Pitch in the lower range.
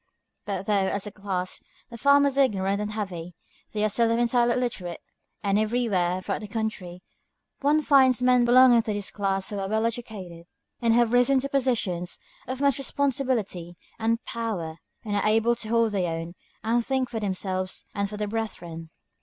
No: high, 215 Hz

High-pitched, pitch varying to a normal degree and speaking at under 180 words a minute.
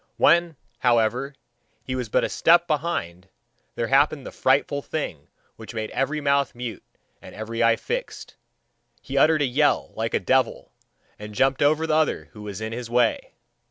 No: low, 130 Hz; average, 4.8 semitones; average, 170 wpm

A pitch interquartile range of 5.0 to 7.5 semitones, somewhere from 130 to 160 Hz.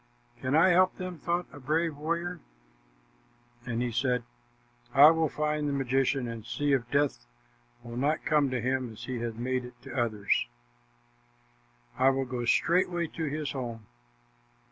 No: average, 4.2 semitones; low, 135 Hz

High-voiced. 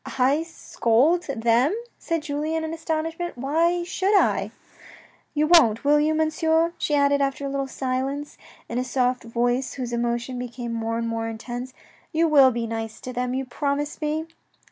Yes: very high, 275 Hz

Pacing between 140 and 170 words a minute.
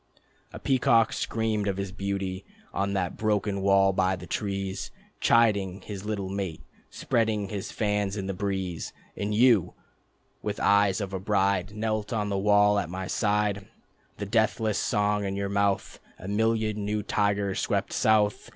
Yes: average, 160 wpm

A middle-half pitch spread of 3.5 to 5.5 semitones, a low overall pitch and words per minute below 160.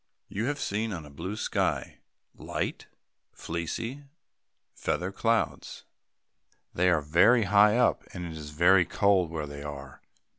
Yes: average, 5.1 semitones; very low, 90 Hz; average, 140 wpm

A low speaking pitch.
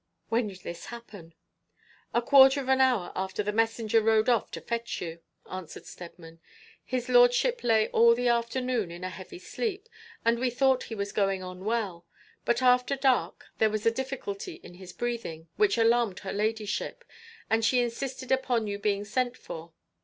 No: high, 225 Hz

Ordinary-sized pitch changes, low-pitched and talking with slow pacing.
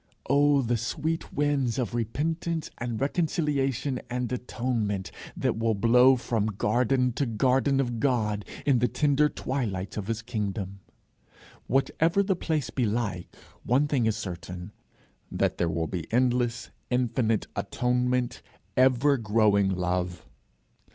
Yes: average, 4.1 semitones; low, 120 Hz; slow, 130 wpm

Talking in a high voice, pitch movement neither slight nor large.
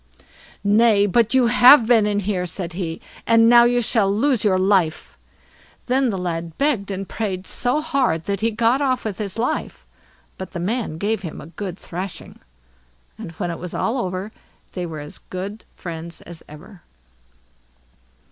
Yes: high, 200 Hz; average, 4.5 semitones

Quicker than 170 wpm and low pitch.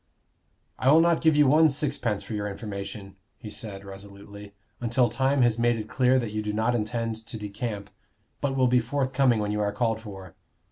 Yes: average, 195 wpm; low, 115 Hz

